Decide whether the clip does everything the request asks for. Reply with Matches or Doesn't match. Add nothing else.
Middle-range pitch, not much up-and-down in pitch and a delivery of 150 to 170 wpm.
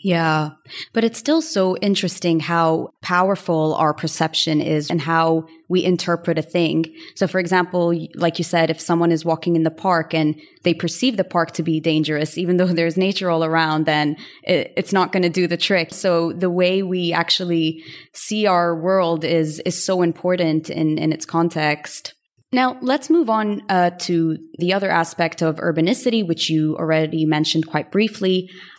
Doesn't match